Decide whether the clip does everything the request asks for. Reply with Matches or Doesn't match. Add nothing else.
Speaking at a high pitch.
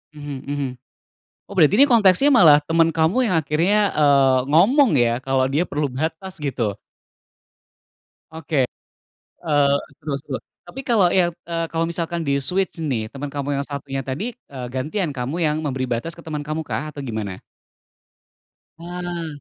Doesn't match